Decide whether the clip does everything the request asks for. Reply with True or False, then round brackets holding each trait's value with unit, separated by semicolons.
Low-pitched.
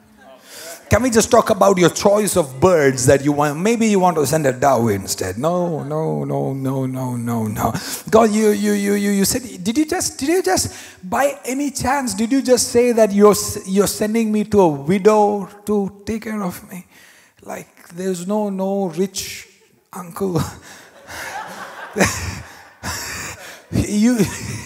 False (200 Hz)